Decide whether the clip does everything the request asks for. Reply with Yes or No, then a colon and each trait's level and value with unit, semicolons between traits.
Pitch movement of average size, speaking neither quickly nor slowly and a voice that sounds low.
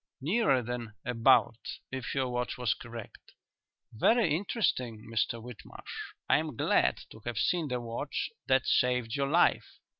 Yes: average, 3.2 semitones; average, 145 wpm; low, 125 Hz